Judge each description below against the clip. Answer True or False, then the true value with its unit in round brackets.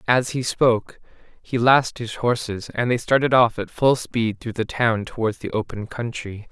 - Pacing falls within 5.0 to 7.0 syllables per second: False (4.6 syllables/s)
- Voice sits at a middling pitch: False (115 Hz)